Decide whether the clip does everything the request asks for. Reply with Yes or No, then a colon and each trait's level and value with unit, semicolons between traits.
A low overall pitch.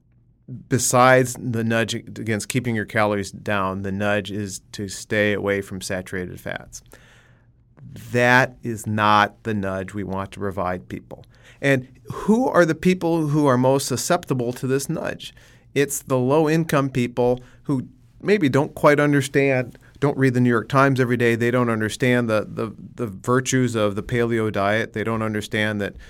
Yes: low, 120 Hz